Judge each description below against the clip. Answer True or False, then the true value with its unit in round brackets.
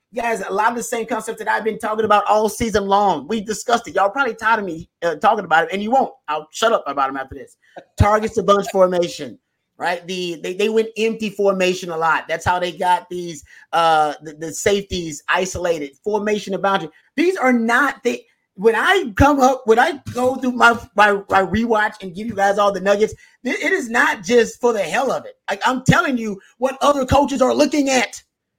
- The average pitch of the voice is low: False (215 Hz)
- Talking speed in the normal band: False (225 wpm)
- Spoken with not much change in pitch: False (4.6 semitones)